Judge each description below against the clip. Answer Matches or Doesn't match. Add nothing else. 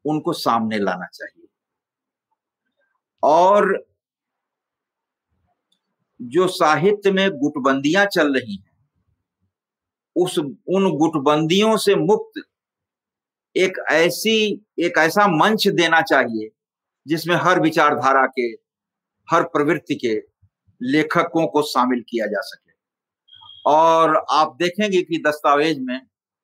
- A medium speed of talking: Doesn't match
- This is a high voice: Doesn't match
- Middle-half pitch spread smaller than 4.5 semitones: Doesn't match